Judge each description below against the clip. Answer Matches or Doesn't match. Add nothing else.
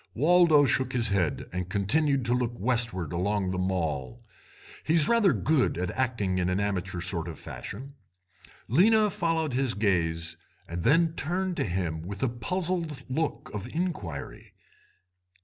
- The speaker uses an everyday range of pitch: Doesn't match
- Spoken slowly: Doesn't match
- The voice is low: Matches